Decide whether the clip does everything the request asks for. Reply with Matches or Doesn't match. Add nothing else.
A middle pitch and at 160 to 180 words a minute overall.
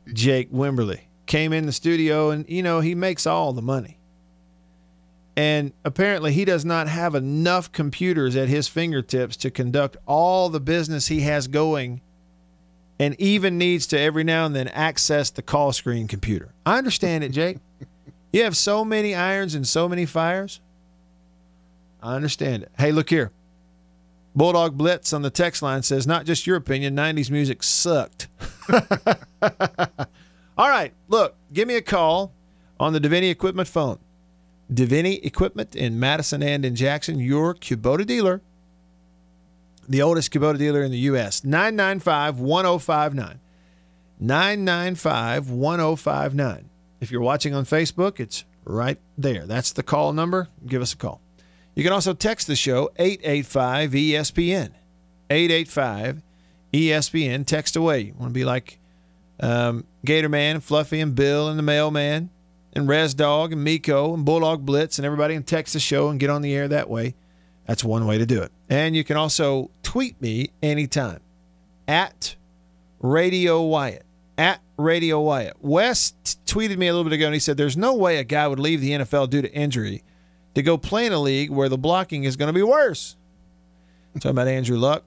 Matches